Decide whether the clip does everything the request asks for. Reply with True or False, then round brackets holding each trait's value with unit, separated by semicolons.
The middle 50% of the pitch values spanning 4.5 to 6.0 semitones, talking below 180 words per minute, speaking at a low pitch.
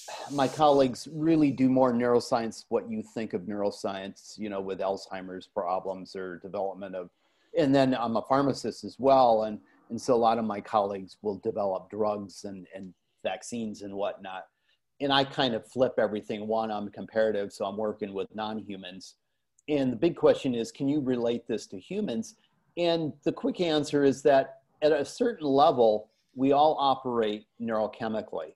True (5.3 semitones; 170 wpm; 115 Hz)